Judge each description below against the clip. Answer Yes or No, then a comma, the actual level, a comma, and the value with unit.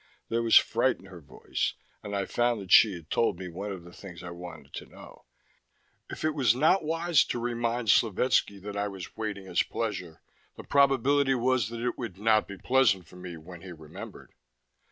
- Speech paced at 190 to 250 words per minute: Yes, average, 200 wpm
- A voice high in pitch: No, low, 105 Hz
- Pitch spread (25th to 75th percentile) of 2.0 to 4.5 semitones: No, average, 5.0 semitones